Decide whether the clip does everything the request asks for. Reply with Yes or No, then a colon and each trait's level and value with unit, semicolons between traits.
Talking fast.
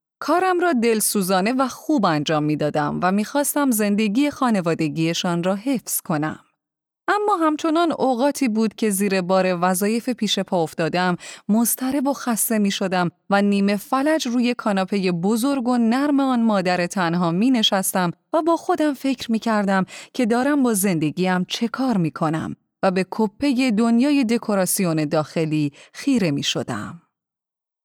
No: average, 145 wpm